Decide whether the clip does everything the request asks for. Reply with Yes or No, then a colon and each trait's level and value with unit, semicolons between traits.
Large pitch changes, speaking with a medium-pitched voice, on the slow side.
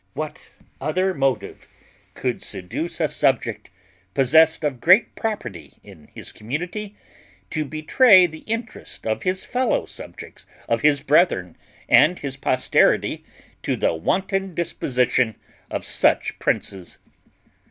Yes: wide, 6.7 semitones; medium, 155 Hz; slow, 120 wpm